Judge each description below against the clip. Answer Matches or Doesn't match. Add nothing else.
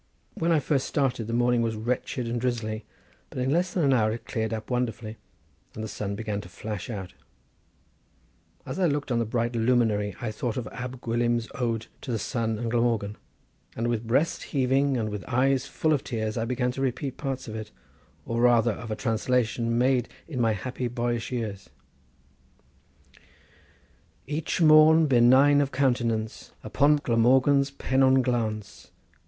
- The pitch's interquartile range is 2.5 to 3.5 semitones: Matches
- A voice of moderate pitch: Doesn't match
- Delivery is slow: Doesn't match